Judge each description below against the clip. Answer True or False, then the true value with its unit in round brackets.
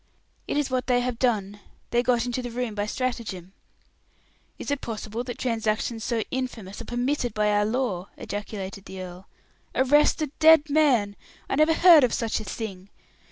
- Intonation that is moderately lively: True (3.7 semitones)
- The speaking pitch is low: False (235 Hz)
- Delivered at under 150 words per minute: False (175 wpm)